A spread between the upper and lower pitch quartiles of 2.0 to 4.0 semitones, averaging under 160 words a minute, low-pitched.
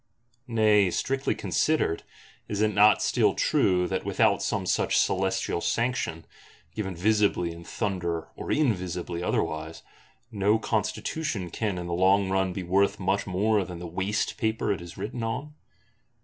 Yes: average, 3.4 semitones; average, 150 wpm; very low, 95 Hz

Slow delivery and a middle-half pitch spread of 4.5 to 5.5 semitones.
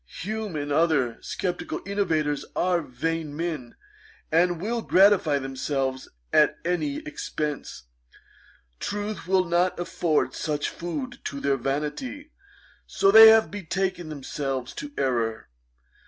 Yes: slow, 115 wpm; average, 5.2 semitones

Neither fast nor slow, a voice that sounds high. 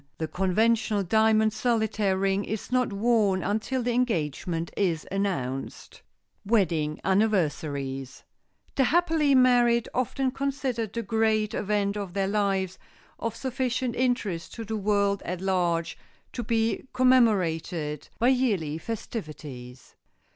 No: slow, 120 wpm; high, 210 Hz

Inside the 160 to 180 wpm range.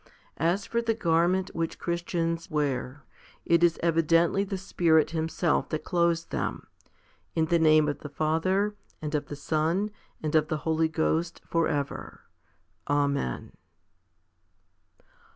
No: slow, 135 wpm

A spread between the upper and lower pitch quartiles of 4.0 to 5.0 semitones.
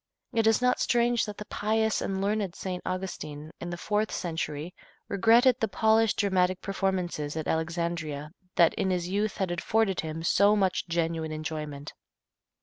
Yes: average, 4.4 semitones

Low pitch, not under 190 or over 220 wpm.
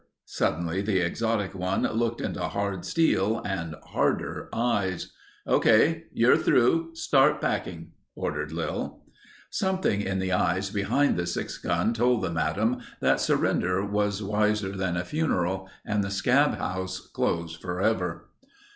No: low, 100 Hz; slow, 135 wpm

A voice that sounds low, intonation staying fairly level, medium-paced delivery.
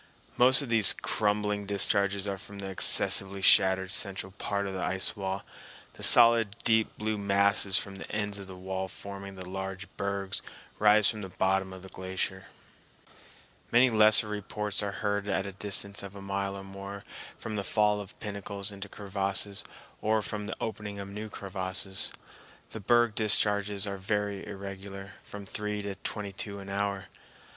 Yes: low, 100 Hz; narrow, 1.2 semitones; average, 170 wpm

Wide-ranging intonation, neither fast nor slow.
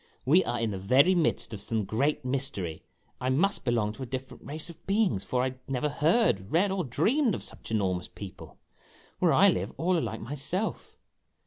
Yes: wide, 7.4 semitones; average, 195 wpm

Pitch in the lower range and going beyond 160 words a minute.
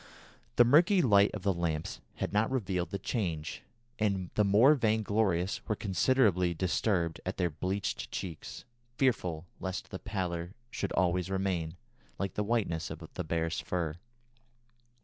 No: very low, 95 Hz; average, 145 wpm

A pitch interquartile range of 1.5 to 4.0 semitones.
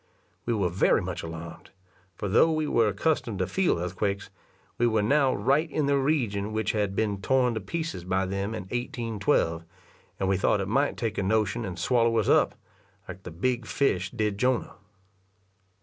No: average, 4.8 semitones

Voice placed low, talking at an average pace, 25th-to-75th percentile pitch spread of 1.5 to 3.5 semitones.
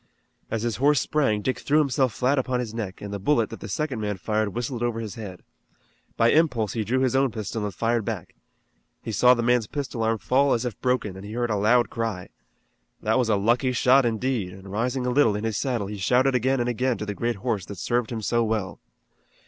No: low, 115 Hz; fast, 235 wpm; average, 3.1 semitones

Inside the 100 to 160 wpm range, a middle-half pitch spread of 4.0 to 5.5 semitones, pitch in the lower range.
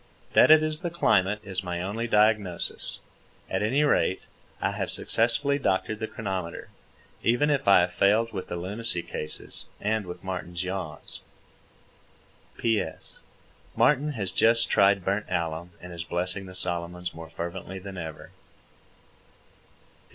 Yes: average, 140 wpm; average, 4.3 semitones; very low, 95 Hz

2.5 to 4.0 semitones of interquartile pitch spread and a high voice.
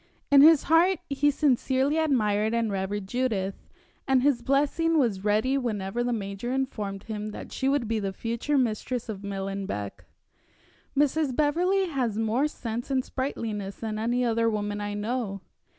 No: average, 4.9 semitones; high, 235 Hz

